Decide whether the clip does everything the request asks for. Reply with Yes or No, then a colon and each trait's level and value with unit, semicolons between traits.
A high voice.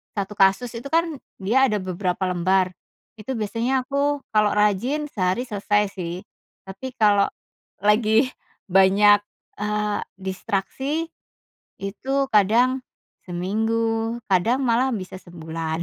Yes: high, 210 Hz